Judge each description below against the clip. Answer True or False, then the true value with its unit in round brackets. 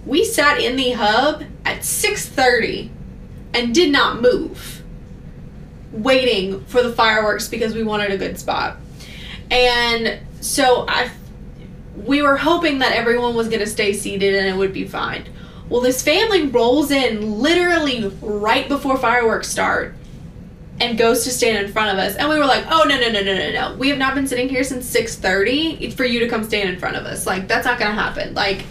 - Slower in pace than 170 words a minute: False (190 wpm)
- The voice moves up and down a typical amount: True (4.3 semitones)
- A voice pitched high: True (245 Hz)